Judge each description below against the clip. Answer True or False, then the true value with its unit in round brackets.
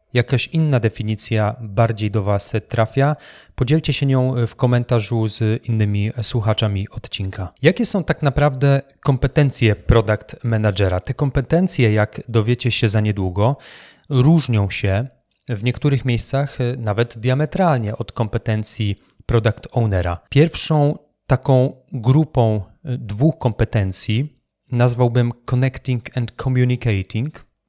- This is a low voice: True (120 Hz)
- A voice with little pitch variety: False (3.8 semitones)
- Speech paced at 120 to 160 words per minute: False (110 wpm)